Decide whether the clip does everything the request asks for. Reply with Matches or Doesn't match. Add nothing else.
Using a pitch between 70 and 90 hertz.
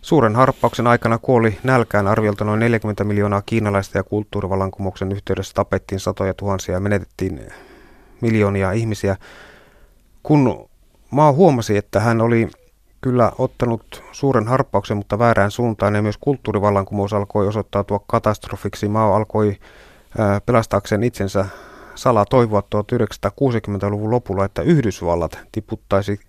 Doesn't match